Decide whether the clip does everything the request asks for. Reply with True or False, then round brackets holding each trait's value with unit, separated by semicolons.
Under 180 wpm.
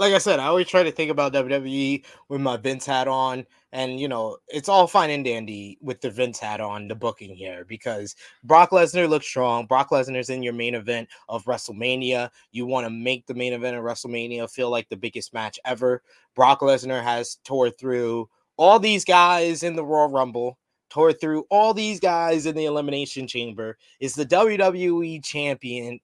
False (195 wpm)